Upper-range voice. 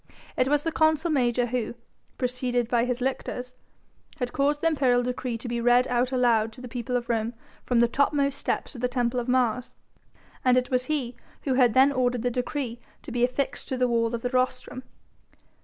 Yes: very high, 250 Hz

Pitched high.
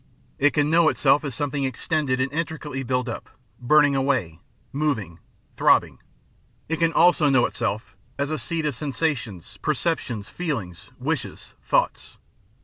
No: medium, 140 Hz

